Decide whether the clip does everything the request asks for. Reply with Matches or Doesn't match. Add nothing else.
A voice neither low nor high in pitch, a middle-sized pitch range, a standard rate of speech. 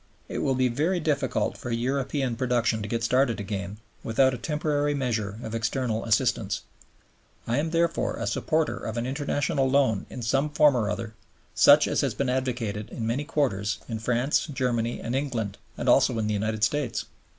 Doesn't match